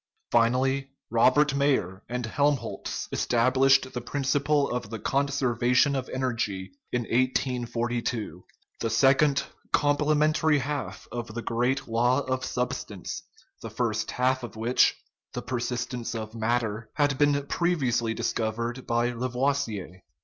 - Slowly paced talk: Yes, slow, 115 wpm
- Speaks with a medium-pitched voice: No, low, 125 Hz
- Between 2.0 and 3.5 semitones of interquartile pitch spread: Yes, average, 2.9 semitones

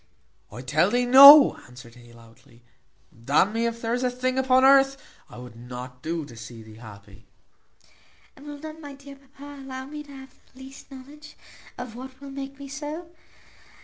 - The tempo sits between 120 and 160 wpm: No, average, 190 wpm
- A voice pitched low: No, very high, 255 Hz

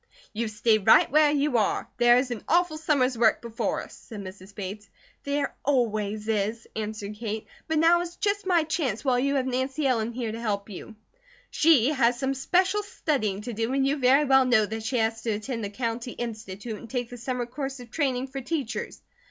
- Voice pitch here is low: No, high, 245 Hz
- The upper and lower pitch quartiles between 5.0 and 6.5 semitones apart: No, average, 4.0 semitones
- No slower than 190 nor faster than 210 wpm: Yes, fast, 205 wpm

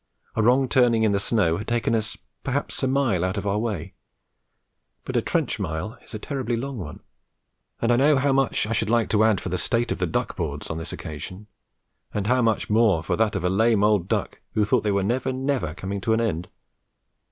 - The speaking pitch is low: Yes, low, 110 Hz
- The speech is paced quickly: Yes, fast, 230 wpm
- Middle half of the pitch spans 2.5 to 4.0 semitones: Yes, average, 3.6 semitones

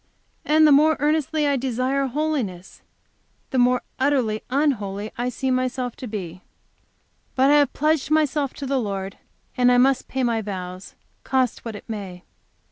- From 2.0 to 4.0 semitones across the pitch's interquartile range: No, average, 4.7 semitones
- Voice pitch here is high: Yes, very high, 255 Hz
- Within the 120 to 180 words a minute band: Yes, average, 160 wpm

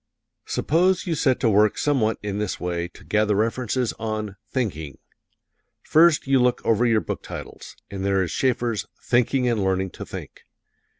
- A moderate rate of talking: Yes, average, 165 wpm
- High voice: No, low, 110 Hz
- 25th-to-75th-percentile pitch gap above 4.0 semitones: Yes, average, 4.4 semitones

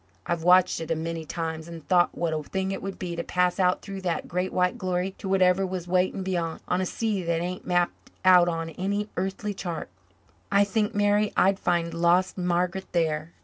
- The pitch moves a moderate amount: No, narrow, 2.0 semitones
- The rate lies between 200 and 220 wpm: Yes, fast, 205 wpm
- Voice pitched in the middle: Yes, medium, 180 Hz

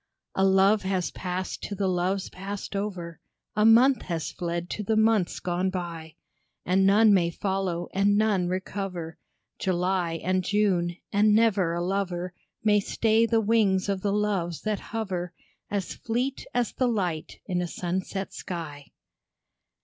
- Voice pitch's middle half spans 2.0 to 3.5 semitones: Yes, average, 2.9 semitones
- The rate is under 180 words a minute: Yes, average, 150 wpm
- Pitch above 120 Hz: Yes, high, 190 Hz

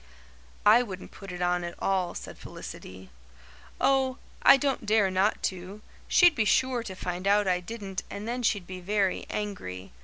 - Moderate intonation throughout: Yes, average, 3.6 semitones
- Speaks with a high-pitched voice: Yes, high, 200 Hz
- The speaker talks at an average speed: Yes, average, 175 wpm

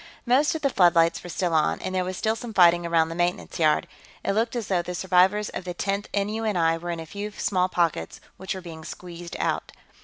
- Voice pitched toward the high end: No, medium, 180 Hz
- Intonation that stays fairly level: No, average, 3.2 semitones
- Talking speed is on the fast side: Yes, fast, 225 wpm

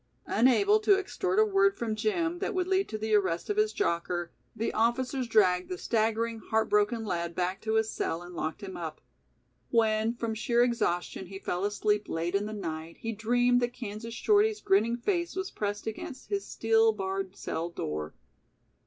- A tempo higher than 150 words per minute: Yes, average, 185 wpm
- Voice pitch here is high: Yes, high, 220 Hz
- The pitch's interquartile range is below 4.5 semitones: No, average, 4.9 semitones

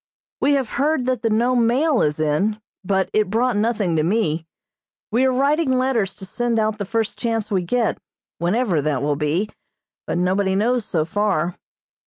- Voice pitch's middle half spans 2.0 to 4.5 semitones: No, average, 5.2 semitones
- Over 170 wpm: Yes, average, 180 wpm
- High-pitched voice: Yes, high, 215 Hz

